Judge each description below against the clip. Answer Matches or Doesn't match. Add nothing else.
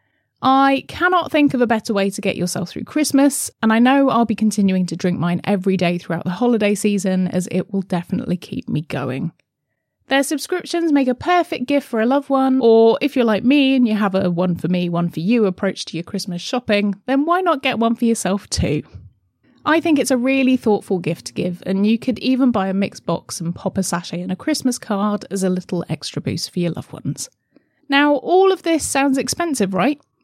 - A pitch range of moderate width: Doesn't match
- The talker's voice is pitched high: Matches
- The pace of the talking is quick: Matches